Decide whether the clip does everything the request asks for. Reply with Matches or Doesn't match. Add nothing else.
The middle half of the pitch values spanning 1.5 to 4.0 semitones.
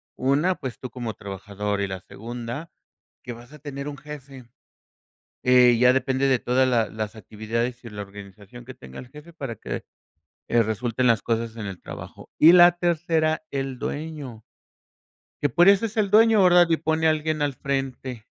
Doesn't match